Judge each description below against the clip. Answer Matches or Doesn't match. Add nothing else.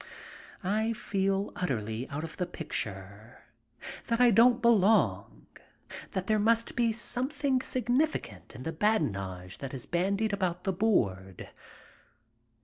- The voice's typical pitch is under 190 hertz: Doesn't match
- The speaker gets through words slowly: Matches